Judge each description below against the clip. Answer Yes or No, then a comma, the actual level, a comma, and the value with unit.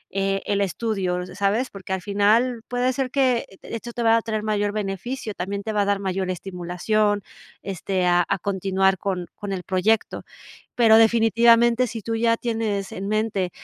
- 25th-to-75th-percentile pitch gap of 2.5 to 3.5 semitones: Yes, average, 2.9 semitones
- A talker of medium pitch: No, high, 205 Hz